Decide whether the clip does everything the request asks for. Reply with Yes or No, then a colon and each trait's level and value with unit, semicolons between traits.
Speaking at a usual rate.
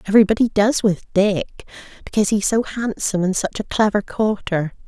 Yes: average, 160 wpm